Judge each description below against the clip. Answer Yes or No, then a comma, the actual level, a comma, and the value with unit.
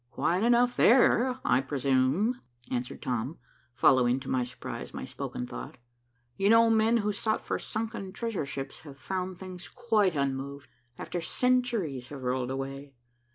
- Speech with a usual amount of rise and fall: No, wide, 8.9 semitones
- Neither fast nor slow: Yes, average, 150 wpm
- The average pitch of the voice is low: No, medium, 165 Hz